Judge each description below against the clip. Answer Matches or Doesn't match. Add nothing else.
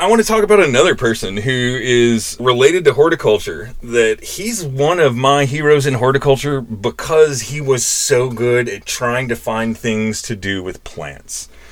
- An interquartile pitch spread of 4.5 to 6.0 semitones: Matches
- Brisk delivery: Doesn't match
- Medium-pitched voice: Doesn't match